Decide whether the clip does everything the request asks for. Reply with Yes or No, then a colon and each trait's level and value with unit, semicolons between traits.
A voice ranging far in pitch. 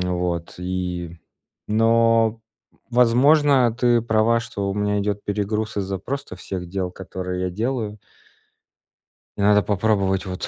No: average, 3.7 semitones